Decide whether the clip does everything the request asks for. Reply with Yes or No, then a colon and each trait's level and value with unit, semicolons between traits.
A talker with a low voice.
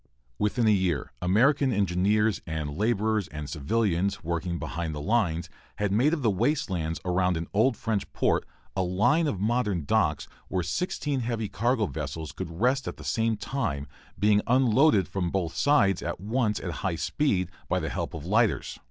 Yes: low, 100 Hz